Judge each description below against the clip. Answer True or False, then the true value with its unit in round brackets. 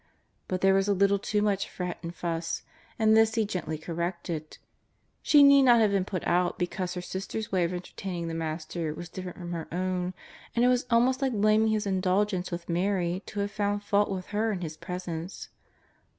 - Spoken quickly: True (210 wpm)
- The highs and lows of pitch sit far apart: False (3.1 semitones)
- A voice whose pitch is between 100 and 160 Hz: False (185 Hz)